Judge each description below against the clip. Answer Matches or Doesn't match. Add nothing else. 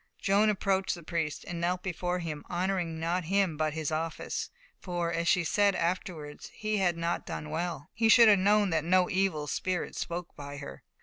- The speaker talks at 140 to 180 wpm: Doesn't match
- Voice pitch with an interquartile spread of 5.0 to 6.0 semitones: Doesn't match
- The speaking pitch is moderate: Matches